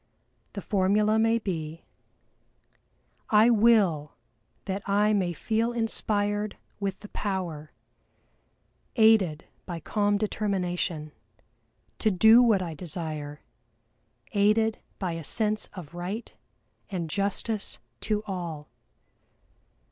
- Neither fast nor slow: No, slow, 100 wpm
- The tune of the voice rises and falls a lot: No, average, 3.7 semitones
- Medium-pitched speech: No, high, 200 Hz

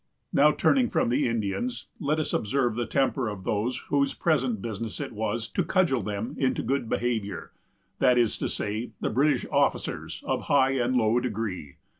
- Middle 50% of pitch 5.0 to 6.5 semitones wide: No, average, 4.2 semitones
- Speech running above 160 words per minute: Yes, average, 175 wpm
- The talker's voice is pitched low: Yes, low, 120 Hz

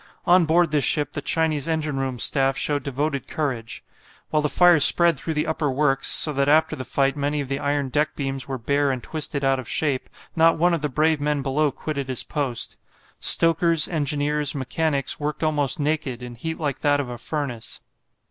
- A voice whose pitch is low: No, medium, 145 Hz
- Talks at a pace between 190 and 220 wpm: Yes, average, 200 wpm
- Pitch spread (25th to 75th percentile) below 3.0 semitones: Yes, narrow, 2.4 semitones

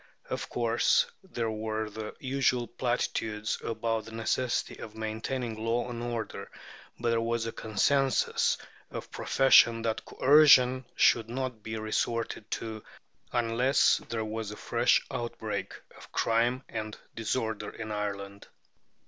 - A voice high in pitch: No, low, 115 Hz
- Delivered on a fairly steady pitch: Yes, narrow, 1.8 semitones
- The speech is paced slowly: Yes, slow, 130 wpm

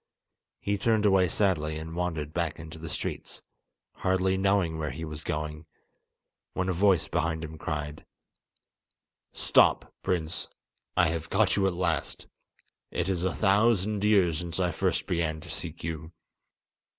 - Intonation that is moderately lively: Yes, average, 3.2 semitones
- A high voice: No, very low, 85 Hz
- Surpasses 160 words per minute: No, average, 150 wpm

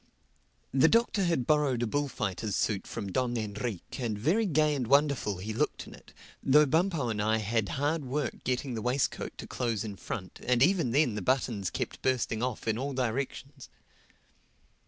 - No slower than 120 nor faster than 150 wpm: No, average, 180 wpm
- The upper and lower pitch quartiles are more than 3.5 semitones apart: Yes, average, 4.8 semitones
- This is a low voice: Yes, low, 125 Hz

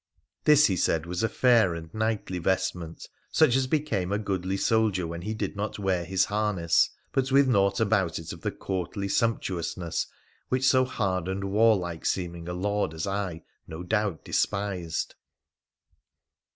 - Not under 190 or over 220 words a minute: No, average, 165 wpm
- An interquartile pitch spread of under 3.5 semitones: No, average, 3.8 semitones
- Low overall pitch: Yes, very low, 95 Hz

